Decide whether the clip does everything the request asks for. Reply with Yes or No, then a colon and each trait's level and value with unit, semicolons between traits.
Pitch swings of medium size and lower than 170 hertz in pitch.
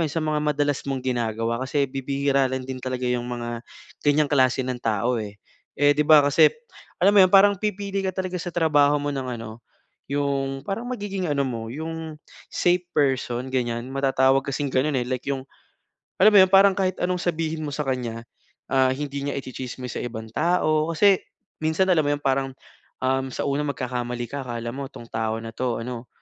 Yes: average, 3.8 semitones; low, 135 Hz